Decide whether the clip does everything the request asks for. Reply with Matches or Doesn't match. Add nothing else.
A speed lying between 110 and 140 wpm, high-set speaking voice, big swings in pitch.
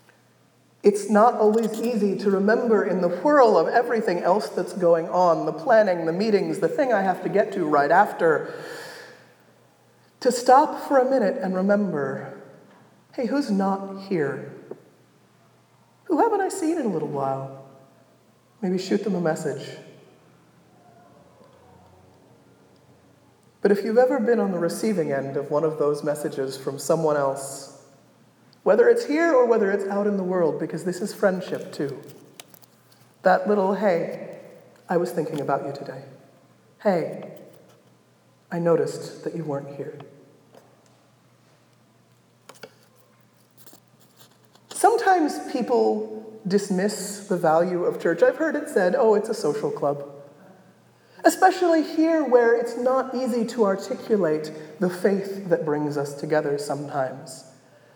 Matches